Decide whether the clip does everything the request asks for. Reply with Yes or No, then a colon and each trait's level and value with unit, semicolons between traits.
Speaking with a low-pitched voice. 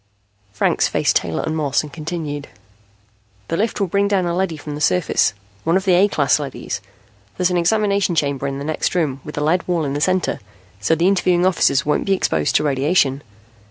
No: medium, 160 Hz